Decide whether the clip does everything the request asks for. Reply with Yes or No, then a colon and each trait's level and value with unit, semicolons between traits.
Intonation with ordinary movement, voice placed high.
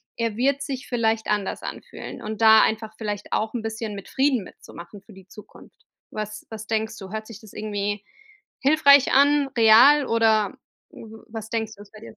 No: narrow, 1.9 semitones; high, 220 Hz